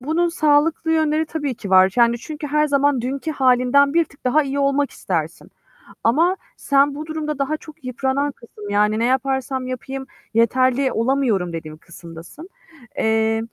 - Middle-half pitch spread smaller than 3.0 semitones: No, average, 4.4 semitones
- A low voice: No, very high, 270 Hz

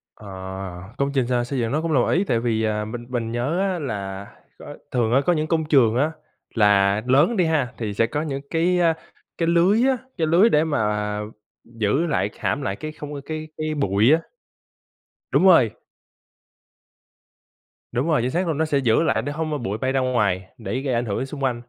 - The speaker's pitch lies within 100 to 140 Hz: Yes, low, 135 Hz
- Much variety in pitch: Yes, wide, 5.7 semitones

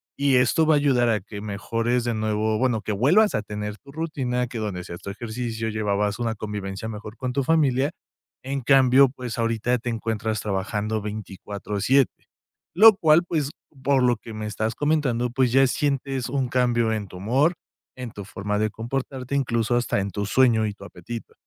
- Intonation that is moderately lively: Yes, average, 3.8 semitones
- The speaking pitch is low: Yes, low, 115 Hz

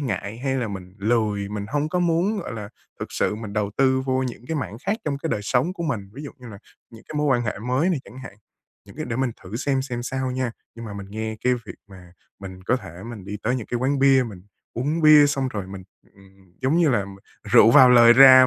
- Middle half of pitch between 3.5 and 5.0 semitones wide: Yes, average, 4.7 semitones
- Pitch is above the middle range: No, low, 125 Hz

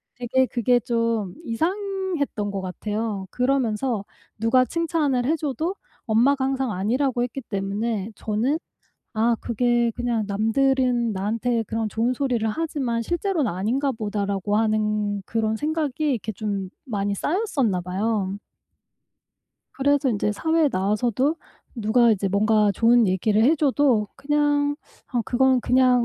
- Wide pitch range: No, average, 4.3 semitones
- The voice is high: Yes, high, 235 Hz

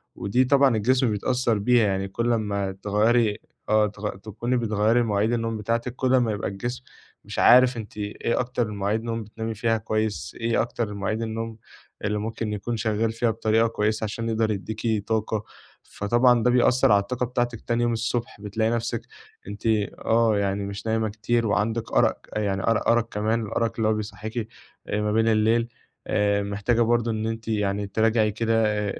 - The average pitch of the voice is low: Yes, low, 110 Hz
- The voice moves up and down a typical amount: No, narrow, 1.9 semitones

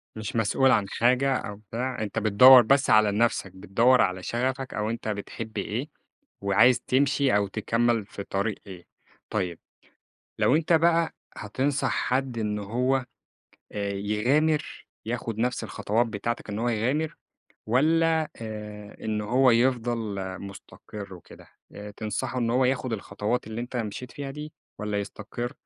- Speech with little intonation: No, average, 3.7 semitones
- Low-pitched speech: Yes, low, 115 Hz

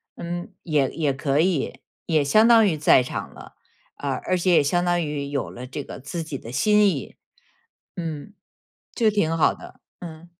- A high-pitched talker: No, medium, 160 Hz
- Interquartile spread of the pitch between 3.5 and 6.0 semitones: Yes, average, 4.0 semitones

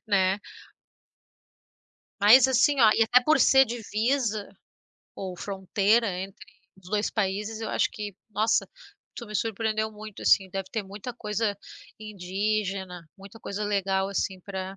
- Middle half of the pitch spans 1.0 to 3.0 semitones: Yes, narrow, 2.4 semitones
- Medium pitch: No, high, 210 Hz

